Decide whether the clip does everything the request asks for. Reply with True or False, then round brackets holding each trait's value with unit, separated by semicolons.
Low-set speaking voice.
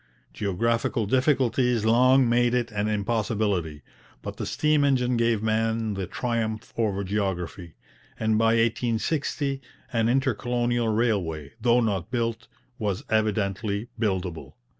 True (115 Hz)